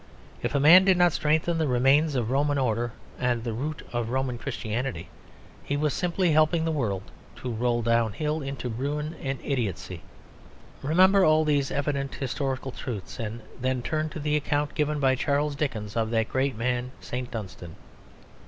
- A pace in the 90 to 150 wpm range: No, average, 170 wpm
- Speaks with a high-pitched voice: No, low, 135 Hz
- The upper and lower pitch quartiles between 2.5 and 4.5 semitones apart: Yes, average, 4.1 semitones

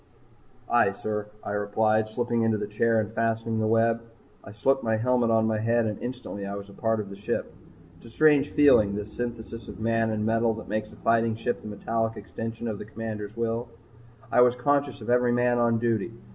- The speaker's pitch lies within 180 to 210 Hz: No, low, 115 Hz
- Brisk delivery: Yes, fast, 215 wpm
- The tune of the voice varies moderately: No, narrow, 1.6 semitones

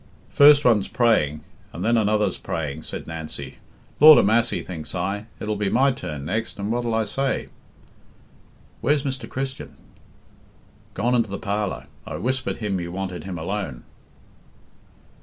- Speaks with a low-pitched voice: Yes, low, 105 Hz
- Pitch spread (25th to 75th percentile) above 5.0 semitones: Yes, wide, 5.6 semitones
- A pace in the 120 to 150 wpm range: Yes, average, 145 wpm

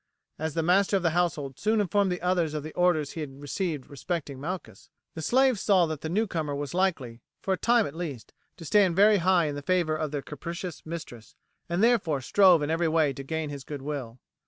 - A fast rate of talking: Yes, fast, 215 wpm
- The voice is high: No, medium, 165 Hz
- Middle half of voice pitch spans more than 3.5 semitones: Yes, average, 4.1 semitones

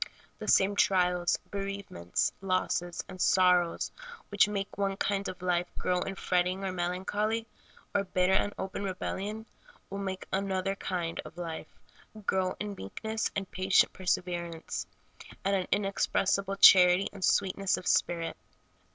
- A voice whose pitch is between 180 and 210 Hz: Yes, high, 190 Hz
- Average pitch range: No, narrow, 1.6 semitones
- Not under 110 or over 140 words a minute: Yes, slow, 135 wpm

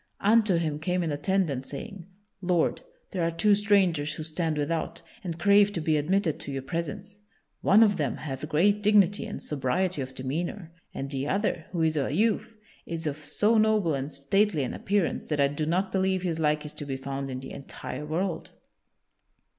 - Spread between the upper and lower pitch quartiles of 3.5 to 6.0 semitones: Yes, average, 5.0 semitones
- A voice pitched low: No, medium, 165 Hz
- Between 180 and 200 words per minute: Yes, average, 190 wpm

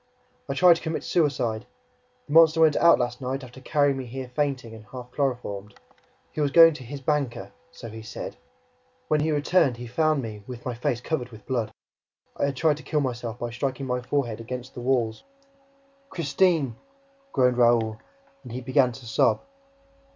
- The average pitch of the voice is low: Yes, low, 130 Hz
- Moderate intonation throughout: Yes, average, 3.5 semitones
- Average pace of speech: Yes, average, 180 wpm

